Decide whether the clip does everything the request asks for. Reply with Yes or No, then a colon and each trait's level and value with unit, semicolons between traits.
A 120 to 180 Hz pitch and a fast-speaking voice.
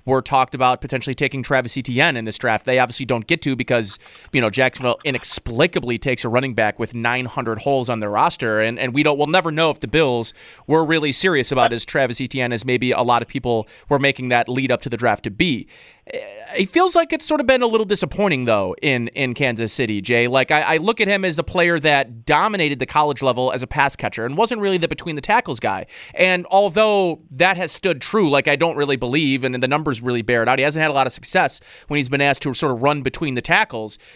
Yes: low, 135 Hz; fast, 250 wpm